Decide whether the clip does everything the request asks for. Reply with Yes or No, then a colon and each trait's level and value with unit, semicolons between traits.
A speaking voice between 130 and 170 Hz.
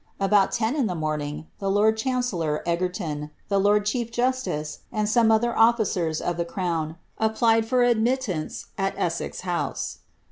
No: high, 205 Hz